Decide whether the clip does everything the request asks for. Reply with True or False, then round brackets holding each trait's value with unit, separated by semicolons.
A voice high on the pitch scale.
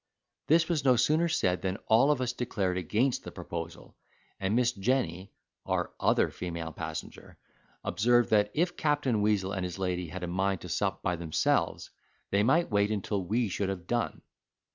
False (105 Hz)